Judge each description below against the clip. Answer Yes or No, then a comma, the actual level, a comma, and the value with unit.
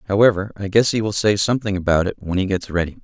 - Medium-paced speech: No, fast, 255 wpm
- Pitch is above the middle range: No, low, 100 Hz